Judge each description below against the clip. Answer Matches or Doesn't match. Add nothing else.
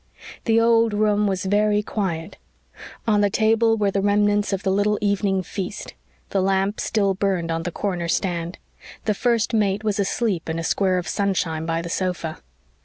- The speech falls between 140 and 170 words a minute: Doesn't match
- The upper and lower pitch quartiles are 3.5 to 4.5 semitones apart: Doesn't match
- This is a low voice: Doesn't match